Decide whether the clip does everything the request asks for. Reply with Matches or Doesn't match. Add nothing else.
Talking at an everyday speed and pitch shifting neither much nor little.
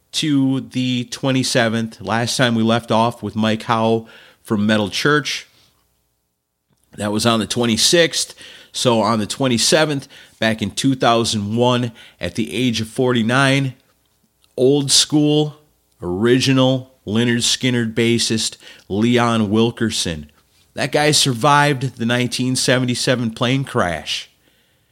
Doesn't match